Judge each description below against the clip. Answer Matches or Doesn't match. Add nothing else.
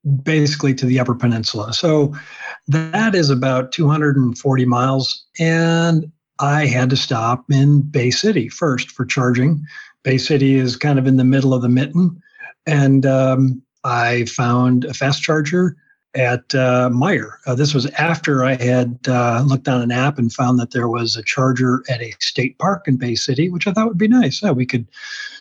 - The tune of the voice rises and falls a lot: Doesn't match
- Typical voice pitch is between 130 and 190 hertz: Matches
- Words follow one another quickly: Doesn't match